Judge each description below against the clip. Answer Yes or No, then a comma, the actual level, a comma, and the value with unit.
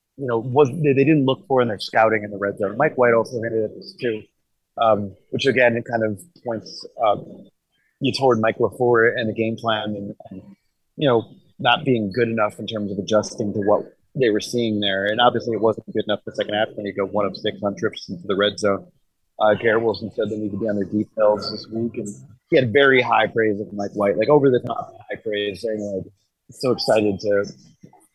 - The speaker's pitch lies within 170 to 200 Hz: No, low, 110 Hz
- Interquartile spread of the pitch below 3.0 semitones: Yes, narrow, 2.6 semitones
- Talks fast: Yes, fast, 240 wpm